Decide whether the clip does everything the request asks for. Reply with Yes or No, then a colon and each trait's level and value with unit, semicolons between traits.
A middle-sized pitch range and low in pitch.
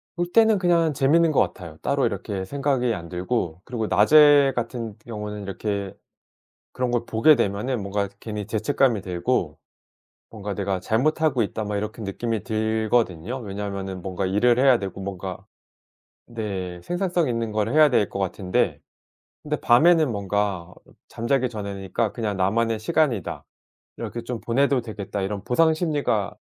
Yes: average, 4.6 semitones; low, 110 Hz